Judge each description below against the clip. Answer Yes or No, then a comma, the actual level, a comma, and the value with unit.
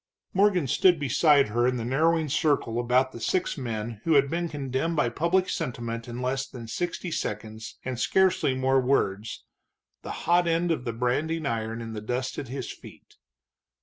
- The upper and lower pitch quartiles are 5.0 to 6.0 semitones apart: Yes, wide, 5.5 semitones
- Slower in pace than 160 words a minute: No, average, 180 wpm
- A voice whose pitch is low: Yes, low, 130 Hz